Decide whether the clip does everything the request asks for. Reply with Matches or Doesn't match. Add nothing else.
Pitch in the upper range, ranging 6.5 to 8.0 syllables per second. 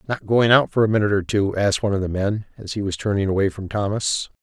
Doesn't match